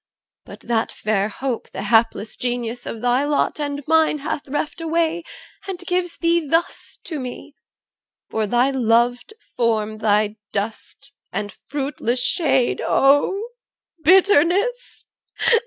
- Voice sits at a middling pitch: No, very high, 265 Hz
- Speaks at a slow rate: Yes, slow, 125 wpm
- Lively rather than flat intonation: Yes, wide, 6.2 semitones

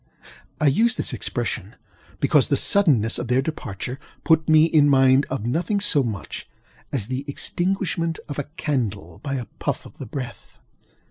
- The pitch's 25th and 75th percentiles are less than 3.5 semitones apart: No, average, 4.6 semitones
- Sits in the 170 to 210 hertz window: No, medium, 140 Hz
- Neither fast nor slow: Yes, average, 160 wpm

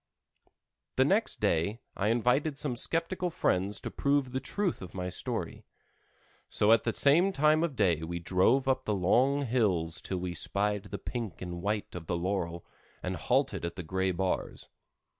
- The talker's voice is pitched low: Yes, low, 105 Hz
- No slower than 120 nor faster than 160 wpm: No, average, 175 wpm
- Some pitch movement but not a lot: No, wide, 6.9 semitones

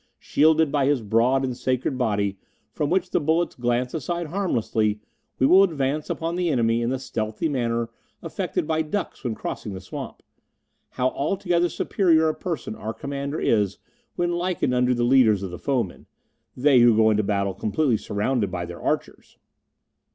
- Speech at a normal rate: Yes, average, 170 wpm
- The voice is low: Yes, low, 130 Hz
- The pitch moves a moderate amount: No, wide, 6.1 semitones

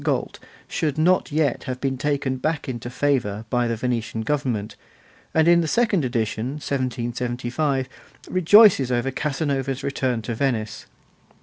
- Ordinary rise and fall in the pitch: Yes, average, 3.6 semitones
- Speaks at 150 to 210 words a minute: No, slow, 135 wpm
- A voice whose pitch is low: Yes, low, 130 Hz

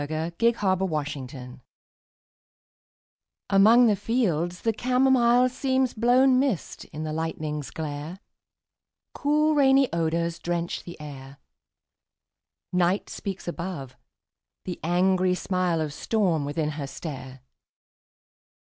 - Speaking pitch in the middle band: Yes, medium, 175 Hz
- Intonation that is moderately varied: No, wide, 7.2 semitones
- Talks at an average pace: No, slow, 110 wpm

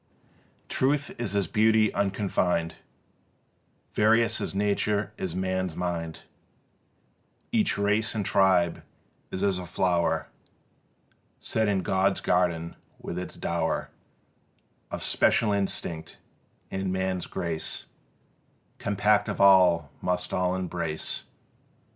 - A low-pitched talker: Yes, very low, 95 Hz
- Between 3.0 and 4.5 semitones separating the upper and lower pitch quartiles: No, narrow, 2.4 semitones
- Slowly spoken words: Yes, slow, 105 wpm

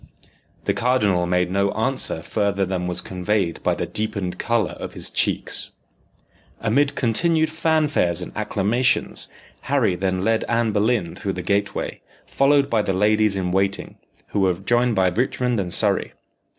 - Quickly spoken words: No, average, 150 wpm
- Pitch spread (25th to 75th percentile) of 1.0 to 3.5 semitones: No, average, 4.2 semitones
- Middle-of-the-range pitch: No, low, 105 Hz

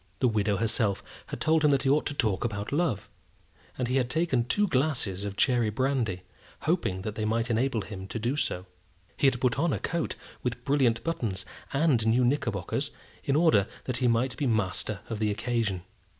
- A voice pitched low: Yes, low, 120 Hz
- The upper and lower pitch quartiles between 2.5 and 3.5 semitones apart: No, average, 4.6 semitones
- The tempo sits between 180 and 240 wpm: Yes, average, 195 wpm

